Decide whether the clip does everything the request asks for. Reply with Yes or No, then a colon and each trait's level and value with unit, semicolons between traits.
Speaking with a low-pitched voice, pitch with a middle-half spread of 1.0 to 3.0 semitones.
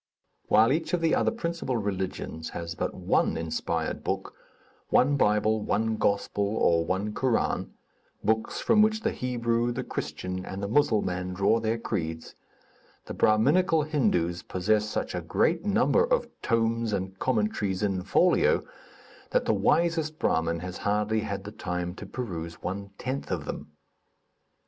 No: low, 105 Hz; wide, 5.6 semitones